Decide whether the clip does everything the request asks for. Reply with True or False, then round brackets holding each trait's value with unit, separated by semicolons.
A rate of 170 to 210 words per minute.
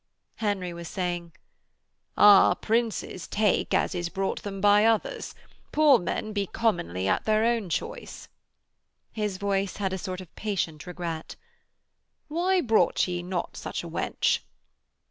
False (140 wpm)